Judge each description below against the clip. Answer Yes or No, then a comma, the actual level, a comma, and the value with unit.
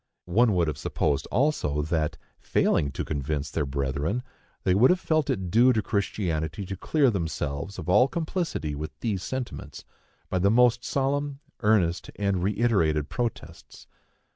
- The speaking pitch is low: Yes, low, 100 Hz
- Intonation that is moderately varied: No, wide, 7.9 semitones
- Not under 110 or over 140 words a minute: No, average, 150 wpm